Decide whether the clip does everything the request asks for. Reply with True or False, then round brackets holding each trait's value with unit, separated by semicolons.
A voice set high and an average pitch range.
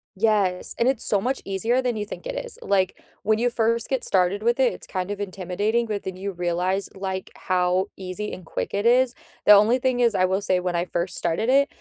True (205 Hz; 4.2 semitones)